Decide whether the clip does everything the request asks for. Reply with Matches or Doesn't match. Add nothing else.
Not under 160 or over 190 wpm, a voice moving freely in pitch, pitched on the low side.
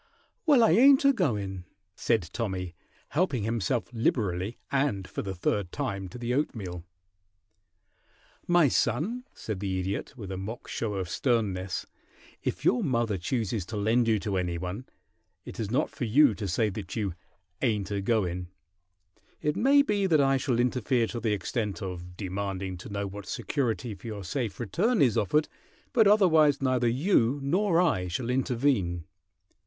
Matches